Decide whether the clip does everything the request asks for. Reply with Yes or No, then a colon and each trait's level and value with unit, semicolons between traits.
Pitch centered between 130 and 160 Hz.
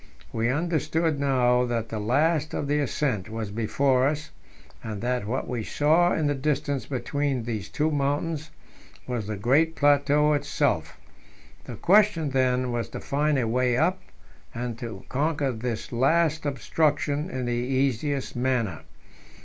Yes: low, 135 Hz